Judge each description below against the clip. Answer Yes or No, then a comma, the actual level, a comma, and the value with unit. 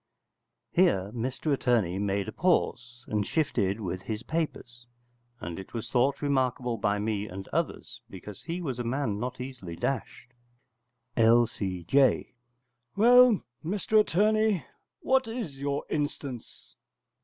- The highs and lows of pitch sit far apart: Yes, wide, 6.7 semitones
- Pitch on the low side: Yes, low, 125 Hz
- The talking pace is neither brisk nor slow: No, slow, 125 wpm